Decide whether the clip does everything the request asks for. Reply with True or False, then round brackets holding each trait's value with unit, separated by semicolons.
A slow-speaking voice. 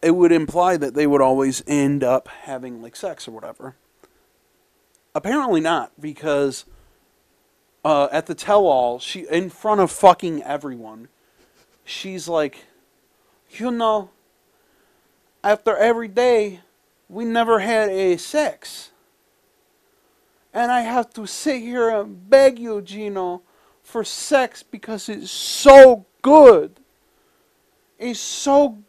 True (120 wpm)